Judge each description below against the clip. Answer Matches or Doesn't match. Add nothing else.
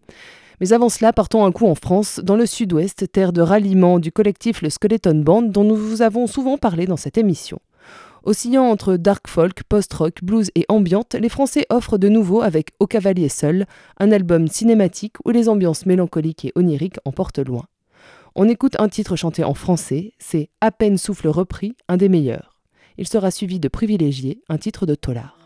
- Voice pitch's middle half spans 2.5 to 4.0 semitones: Doesn't match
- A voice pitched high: Matches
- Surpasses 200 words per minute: Doesn't match